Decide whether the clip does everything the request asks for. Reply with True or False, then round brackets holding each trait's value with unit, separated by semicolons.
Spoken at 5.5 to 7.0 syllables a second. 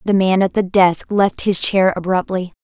False (4.6 syllables/s)